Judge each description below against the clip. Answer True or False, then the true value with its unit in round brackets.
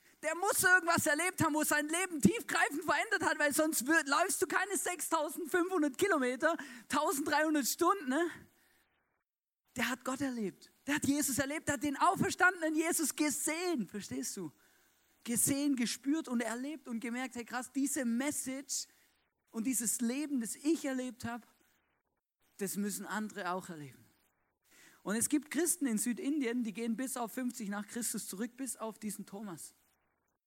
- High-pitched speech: True (265 Hz)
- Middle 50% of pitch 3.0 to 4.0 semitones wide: False (5.5 semitones)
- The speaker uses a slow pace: False (155 wpm)